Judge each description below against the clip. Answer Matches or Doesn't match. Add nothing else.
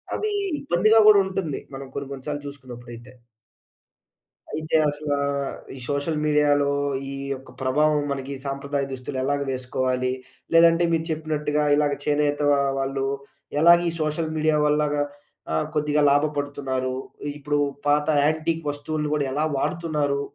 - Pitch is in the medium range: Matches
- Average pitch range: Doesn't match